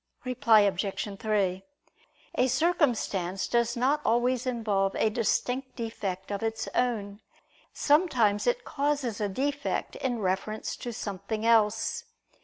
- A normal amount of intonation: Yes, average, 3.9 semitones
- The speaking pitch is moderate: No, high, 225 Hz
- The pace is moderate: No, slow, 120 wpm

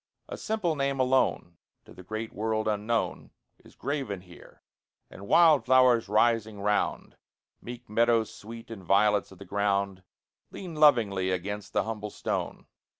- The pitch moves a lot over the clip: No, average, 3.6 semitones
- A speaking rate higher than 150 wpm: No, average, 145 wpm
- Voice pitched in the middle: No, low, 110 Hz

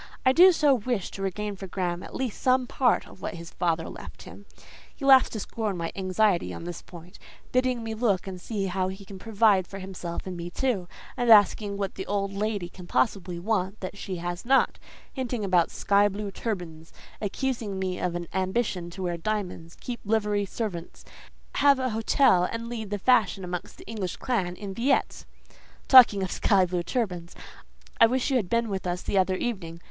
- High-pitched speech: Yes, high, 200 Hz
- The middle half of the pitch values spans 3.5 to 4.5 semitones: Yes, average, 4.0 semitones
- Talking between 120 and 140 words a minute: No, average, 195 wpm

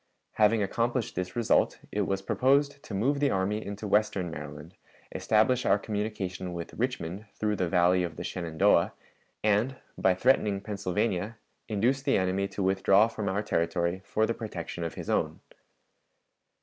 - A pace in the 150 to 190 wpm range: Yes, average, 155 wpm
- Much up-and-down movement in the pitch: No, average, 3.3 semitones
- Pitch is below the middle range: Yes, low, 100 Hz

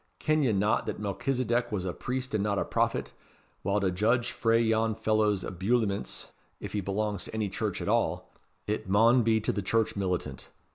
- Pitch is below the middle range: Yes, low, 110 Hz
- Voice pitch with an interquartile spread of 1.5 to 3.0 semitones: Yes, narrow, 2.5 semitones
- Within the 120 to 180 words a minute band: No, average, 190 wpm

